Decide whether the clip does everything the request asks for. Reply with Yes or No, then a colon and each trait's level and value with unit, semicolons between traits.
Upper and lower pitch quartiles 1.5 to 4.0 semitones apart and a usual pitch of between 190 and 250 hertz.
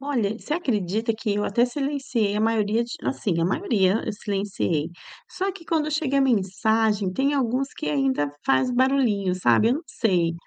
No: wide, 5.5 semitones; high, 225 Hz